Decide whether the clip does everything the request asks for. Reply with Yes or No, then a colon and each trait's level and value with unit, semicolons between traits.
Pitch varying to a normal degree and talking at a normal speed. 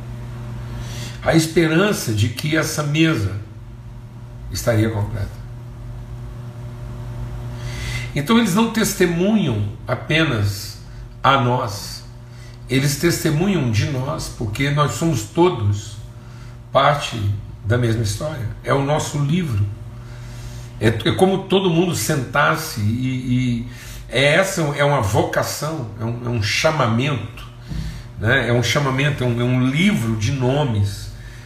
No: average, 4.0 semitones; slow, 115 wpm